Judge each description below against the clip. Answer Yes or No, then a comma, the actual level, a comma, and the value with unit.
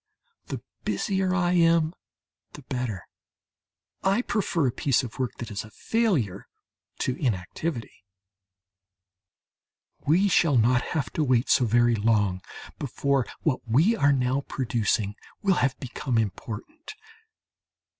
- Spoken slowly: Yes, slow, 125 wpm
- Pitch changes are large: Yes, wide, 6.3 semitones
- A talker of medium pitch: No, low, 130 Hz